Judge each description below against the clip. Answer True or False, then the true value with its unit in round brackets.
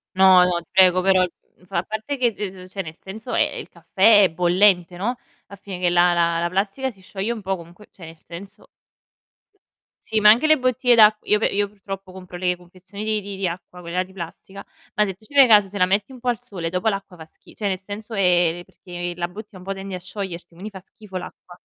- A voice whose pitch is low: False (190 Hz)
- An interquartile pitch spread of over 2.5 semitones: True (2.9 semitones)